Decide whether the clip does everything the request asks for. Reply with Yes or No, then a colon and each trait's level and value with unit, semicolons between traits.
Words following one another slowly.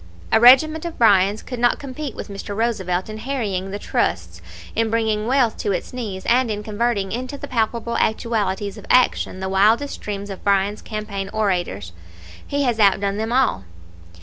No: average, 175 wpm